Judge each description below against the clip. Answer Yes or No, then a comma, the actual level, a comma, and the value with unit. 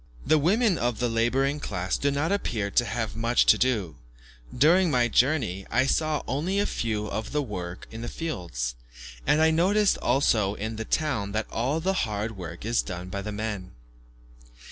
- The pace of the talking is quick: No, average, 180 wpm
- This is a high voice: No, low, 120 Hz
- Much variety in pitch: Yes, wide, 6.4 semitones